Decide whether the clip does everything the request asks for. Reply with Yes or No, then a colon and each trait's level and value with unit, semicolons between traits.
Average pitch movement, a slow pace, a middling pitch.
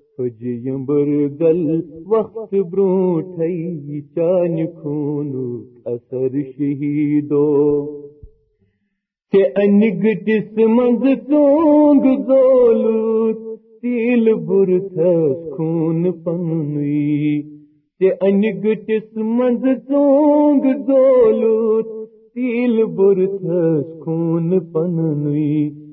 No: wide, 7.0 semitones; slow, 50 wpm; medium, 180 Hz